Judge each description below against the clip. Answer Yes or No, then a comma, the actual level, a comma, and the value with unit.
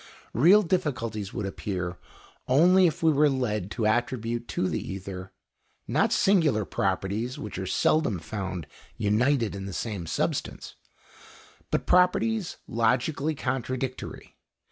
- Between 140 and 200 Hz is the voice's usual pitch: No, low, 120 Hz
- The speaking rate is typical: No, slow, 120 wpm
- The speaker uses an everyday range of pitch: No, wide, 6.9 semitones